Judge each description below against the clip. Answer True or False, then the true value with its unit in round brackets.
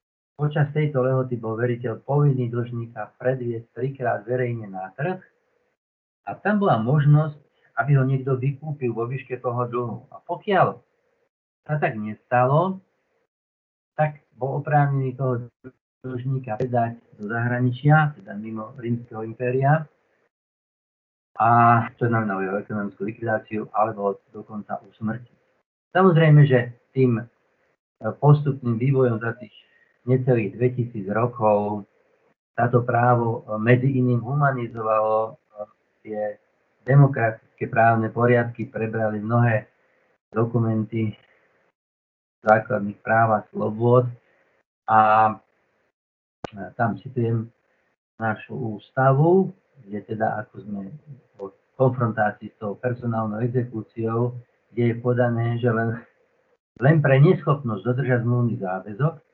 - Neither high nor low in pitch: False (120 Hz)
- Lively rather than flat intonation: False (3.4 semitones)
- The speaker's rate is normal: False (105 wpm)